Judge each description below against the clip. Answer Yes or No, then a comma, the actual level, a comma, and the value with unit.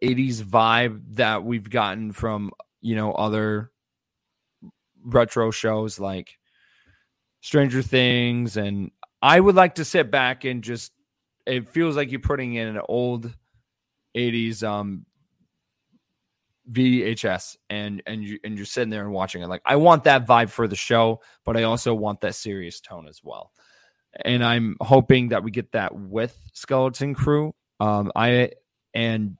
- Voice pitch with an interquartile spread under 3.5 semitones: Yes, average, 2.9 semitones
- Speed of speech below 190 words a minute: Yes, average, 150 wpm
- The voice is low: Yes, low, 115 Hz